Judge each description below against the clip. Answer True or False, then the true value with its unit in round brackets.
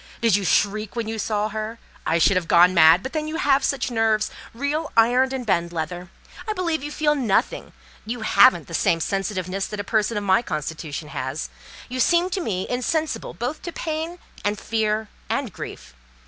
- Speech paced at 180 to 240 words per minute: True (190 wpm)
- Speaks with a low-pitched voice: False (220 Hz)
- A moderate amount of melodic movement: False (6.4 semitones)